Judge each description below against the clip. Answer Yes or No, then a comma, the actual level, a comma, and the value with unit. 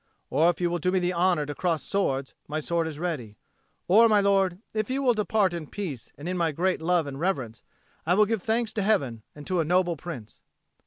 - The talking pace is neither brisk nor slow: No, fast, 230 wpm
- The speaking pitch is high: No, medium, 175 Hz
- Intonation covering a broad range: No, average, 4.3 semitones